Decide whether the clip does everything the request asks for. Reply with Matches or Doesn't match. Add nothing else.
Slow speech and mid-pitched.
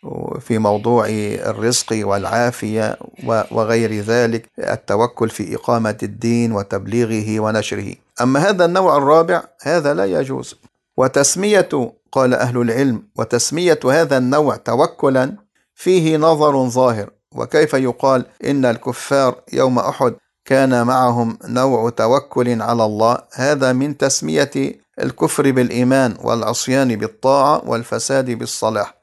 Doesn't match